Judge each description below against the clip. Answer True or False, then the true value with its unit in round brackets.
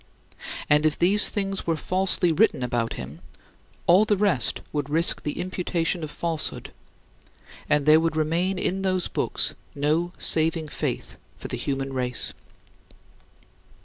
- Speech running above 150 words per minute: False (140 wpm)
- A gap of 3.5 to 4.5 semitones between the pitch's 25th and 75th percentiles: True (3.8 semitones)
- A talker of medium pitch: True (165 Hz)